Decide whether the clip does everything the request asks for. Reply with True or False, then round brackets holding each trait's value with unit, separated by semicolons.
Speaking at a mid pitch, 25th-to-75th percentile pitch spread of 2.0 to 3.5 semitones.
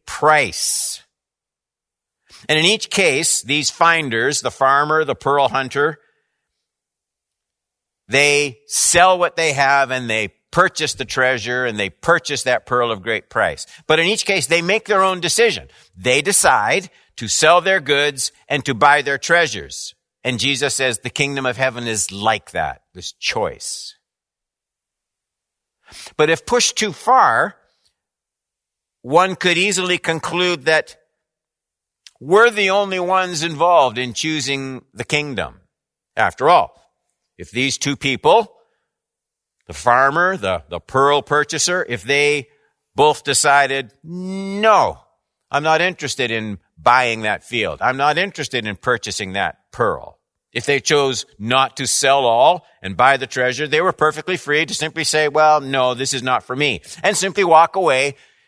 False (145 Hz; 4.9 semitones)